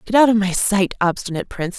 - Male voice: No, female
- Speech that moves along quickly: Yes, fast, 235 wpm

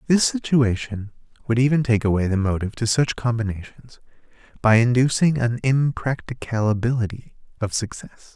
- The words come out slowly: Yes, slow, 120 wpm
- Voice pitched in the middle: No, low, 120 Hz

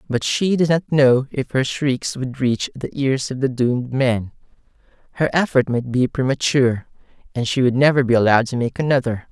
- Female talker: No, male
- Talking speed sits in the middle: Yes, average, 195 wpm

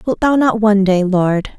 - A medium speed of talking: No, fast, 225 wpm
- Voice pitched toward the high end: Yes, high, 210 Hz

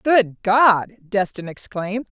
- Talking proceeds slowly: Yes, slow, 110 wpm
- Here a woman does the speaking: Yes, female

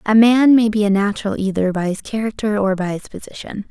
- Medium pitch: No, high, 210 Hz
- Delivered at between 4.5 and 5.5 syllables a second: No, 5.9 syllables/s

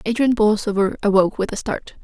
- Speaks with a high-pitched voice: Yes, high, 210 Hz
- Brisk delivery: No, average, 175 wpm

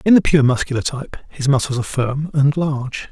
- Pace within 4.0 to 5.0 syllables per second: No, 5.8 syllables/s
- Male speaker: Yes, male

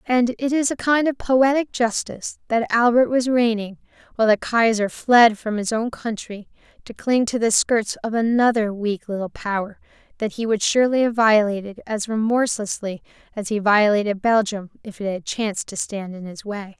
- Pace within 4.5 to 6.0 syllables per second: Yes, 5.0 syllables/s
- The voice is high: Yes, high, 220 Hz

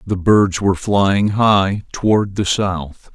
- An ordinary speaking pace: Yes, average, 155 wpm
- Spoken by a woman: No, male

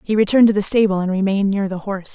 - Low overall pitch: No, high, 200 Hz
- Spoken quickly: Yes, fast, 280 wpm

